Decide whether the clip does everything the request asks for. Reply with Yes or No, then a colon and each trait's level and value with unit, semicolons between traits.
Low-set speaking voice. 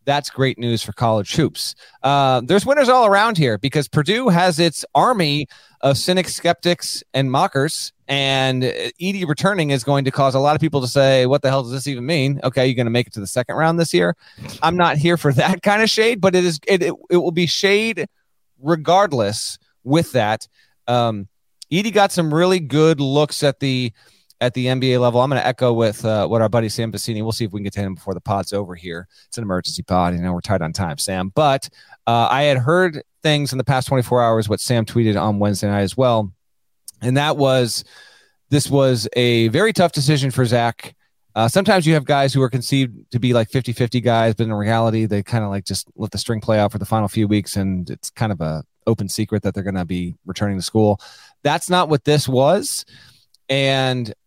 Yes: low, 130 Hz